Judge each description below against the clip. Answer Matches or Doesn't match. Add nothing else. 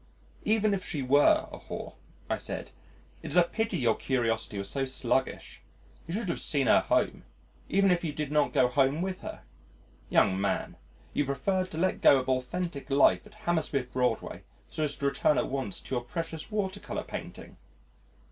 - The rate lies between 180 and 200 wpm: Matches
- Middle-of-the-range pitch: Matches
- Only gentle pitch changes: Doesn't match